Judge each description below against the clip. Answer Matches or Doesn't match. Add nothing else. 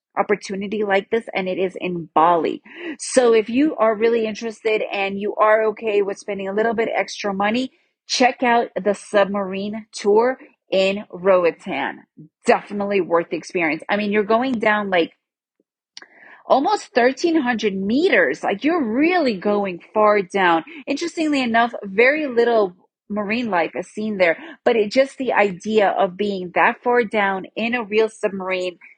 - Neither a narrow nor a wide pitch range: Matches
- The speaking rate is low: Doesn't match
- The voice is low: Doesn't match